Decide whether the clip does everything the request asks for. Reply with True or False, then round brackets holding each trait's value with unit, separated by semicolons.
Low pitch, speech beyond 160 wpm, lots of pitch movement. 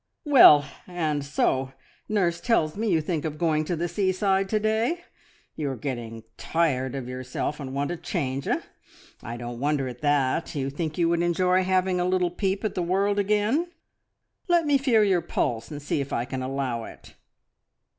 False (165 Hz; 185 wpm; 5.8 semitones)